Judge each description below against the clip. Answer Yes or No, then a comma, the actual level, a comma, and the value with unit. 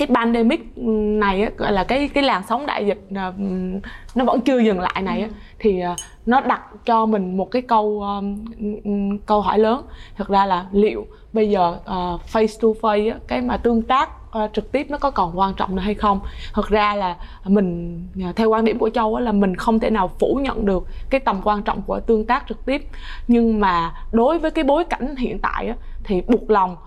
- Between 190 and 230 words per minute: Yes, average, 215 wpm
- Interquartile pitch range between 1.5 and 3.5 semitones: Yes, average, 2.8 semitones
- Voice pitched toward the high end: Yes, high, 215 Hz